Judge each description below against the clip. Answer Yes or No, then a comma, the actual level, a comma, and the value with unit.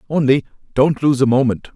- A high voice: No, low, 135 Hz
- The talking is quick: No, average, 170 wpm